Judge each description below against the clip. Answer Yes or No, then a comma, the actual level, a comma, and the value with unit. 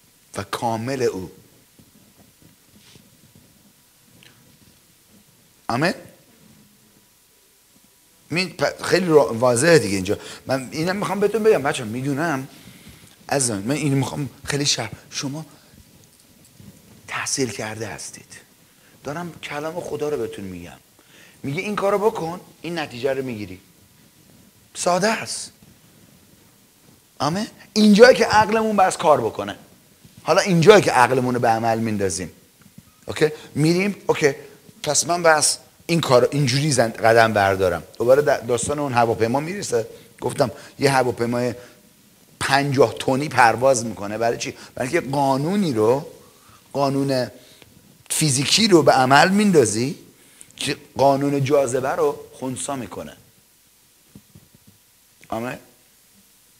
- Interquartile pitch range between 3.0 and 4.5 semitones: No, average, 5.3 semitones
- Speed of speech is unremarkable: No, slow, 105 wpm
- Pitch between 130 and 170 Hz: Yes, medium, 140 Hz